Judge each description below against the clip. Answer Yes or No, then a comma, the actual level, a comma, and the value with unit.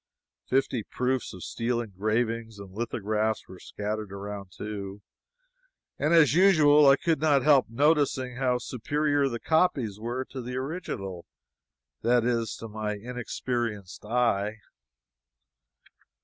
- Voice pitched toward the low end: Yes, low, 120 Hz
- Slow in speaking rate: Yes, slow, 120 wpm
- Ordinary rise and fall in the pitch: Yes, average, 4.3 semitones